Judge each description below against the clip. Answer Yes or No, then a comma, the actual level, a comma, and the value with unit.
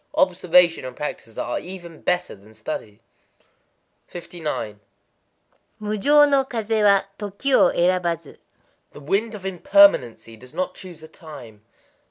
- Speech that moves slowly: Yes, slow, 115 wpm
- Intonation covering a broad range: Yes, wide, 6.5 semitones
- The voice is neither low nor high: Yes, medium, 175 Hz